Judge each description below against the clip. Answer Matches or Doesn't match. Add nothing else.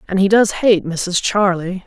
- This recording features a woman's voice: Matches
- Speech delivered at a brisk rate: Doesn't match